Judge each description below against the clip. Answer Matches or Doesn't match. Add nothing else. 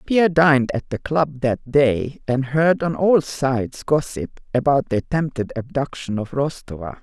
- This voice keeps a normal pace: Matches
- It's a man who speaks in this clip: Doesn't match